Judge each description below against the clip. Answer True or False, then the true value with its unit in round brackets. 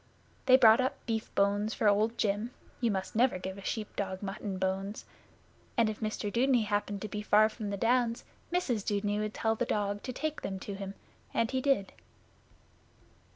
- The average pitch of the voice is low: False (215 Hz)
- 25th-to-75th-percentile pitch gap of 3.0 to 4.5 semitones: False (2.5 semitones)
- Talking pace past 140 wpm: True (190 wpm)